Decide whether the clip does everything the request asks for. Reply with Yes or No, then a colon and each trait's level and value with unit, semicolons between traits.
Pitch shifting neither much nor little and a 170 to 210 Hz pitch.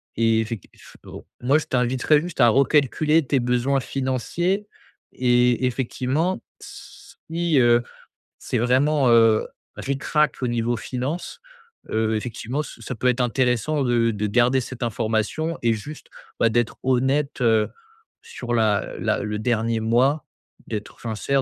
No: average, 3.2 semitones; low, 125 Hz